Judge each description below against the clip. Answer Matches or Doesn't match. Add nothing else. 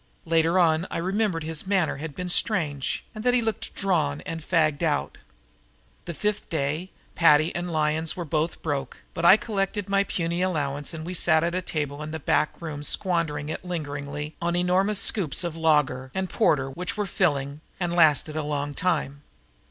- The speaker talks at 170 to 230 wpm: Matches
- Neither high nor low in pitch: Matches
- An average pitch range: Matches